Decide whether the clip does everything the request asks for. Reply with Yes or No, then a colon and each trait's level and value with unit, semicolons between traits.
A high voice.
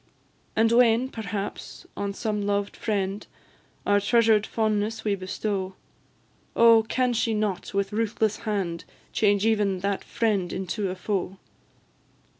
Yes: high, 210 Hz